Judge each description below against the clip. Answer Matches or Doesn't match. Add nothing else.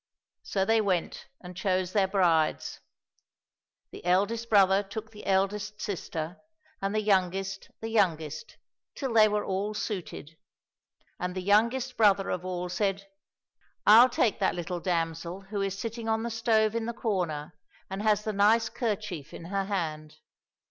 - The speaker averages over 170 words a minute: Doesn't match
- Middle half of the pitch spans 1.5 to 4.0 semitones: Matches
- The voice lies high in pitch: Matches